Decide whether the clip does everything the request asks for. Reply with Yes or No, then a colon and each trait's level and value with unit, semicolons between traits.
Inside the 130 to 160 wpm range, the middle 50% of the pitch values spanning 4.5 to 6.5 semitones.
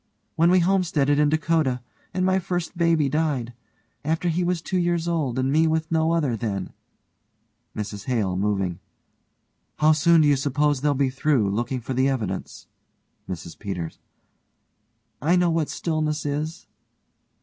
Yes: average, 150 wpm; average, 4.8 semitones